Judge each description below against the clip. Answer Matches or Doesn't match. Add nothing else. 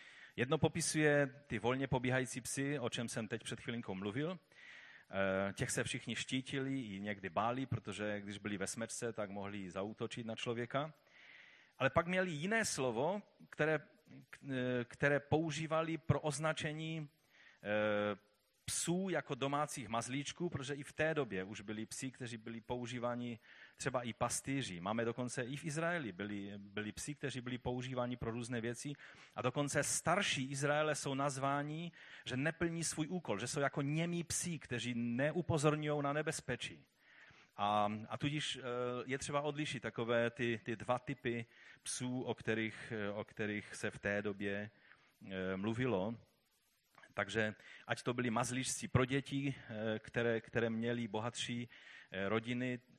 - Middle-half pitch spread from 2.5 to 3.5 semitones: Doesn't match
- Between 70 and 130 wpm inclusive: Doesn't match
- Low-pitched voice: Matches